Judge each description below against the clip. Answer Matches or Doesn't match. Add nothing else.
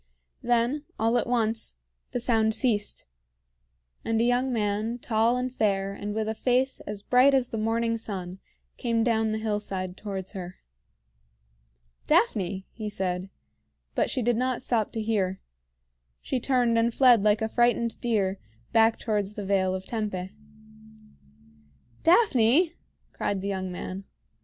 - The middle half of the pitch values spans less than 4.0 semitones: Matches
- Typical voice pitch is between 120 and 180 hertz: Doesn't match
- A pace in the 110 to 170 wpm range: Matches